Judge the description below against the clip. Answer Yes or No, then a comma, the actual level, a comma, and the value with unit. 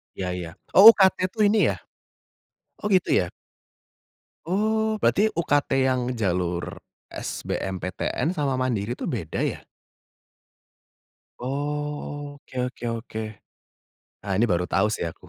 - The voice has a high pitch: No, low, 130 Hz